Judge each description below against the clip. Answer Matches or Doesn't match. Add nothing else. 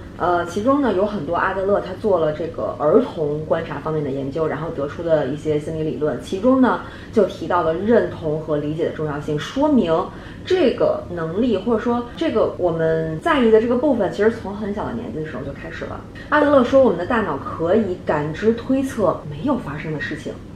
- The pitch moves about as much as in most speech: Doesn't match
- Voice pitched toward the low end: Doesn't match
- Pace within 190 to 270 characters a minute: Doesn't match